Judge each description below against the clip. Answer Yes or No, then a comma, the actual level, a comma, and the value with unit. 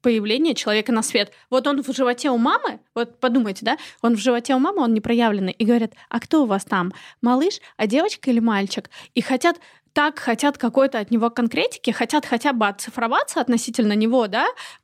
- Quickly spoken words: Yes, fast, 195 wpm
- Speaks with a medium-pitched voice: No, high, 240 Hz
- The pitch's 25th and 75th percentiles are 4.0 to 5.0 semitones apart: No, average, 3.4 semitones